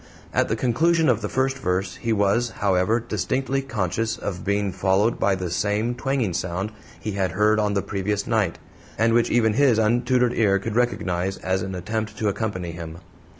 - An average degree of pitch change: Yes, average, 3.6 semitones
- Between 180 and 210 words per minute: Yes, average, 185 wpm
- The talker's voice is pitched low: Yes, low, 105 Hz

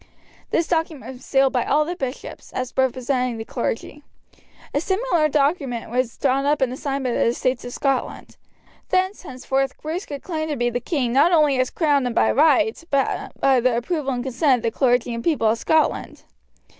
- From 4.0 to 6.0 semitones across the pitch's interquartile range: No, average, 3.5 semitones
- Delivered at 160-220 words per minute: Yes, average, 195 wpm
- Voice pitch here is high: Yes, very high, 270 Hz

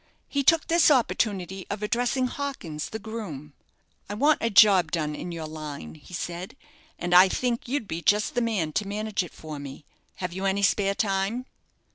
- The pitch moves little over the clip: No, wide, 5.4 semitones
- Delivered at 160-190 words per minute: Yes, average, 185 wpm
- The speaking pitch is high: Yes, high, 195 Hz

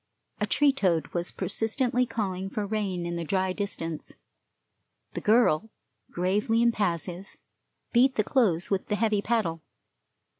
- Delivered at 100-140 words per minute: Yes, slow, 135 wpm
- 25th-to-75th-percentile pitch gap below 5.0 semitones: Yes, average, 4.2 semitones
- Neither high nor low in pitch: No, high, 200 Hz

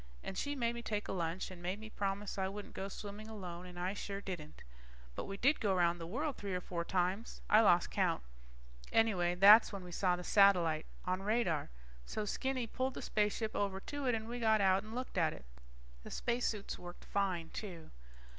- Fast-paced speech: Yes, fast, 210 wpm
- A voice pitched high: Yes, high, 195 Hz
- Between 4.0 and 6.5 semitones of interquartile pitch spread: No, average, 3.5 semitones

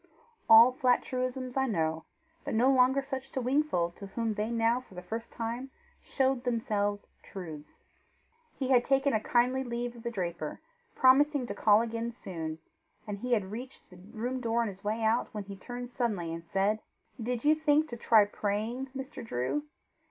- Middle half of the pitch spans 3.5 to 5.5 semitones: Yes, average, 3.8 semitones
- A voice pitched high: Yes, high, 235 Hz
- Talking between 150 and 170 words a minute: No, average, 180 wpm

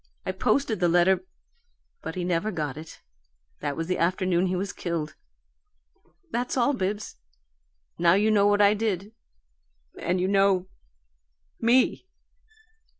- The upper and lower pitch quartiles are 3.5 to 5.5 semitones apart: No, average, 3.1 semitones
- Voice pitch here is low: No, medium, 185 Hz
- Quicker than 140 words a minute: No, slow, 135 wpm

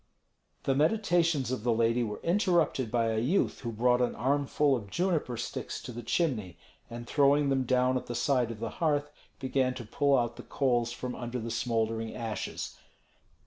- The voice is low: Yes, low, 125 Hz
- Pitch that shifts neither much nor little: Yes, average, 3.5 semitones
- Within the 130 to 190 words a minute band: Yes, average, 185 wpm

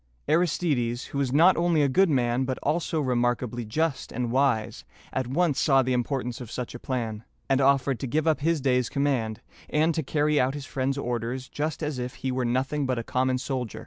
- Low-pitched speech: Yes, low, 130 Hz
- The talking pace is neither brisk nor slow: No, fast, 210 wpm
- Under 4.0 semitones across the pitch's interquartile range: Yes, average, 3.2 semitones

